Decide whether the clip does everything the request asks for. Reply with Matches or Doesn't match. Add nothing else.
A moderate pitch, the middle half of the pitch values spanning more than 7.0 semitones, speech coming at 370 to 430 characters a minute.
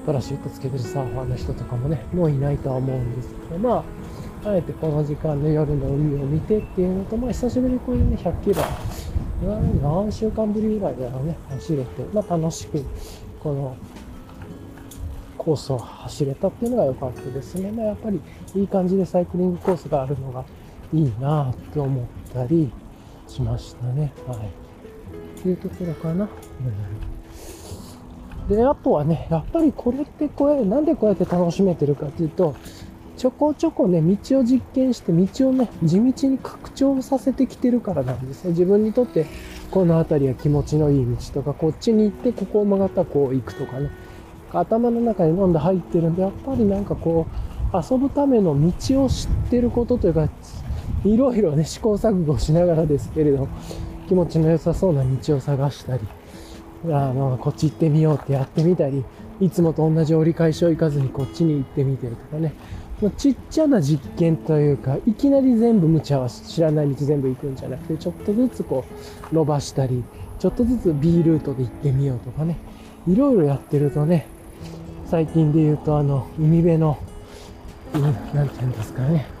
Doesn't match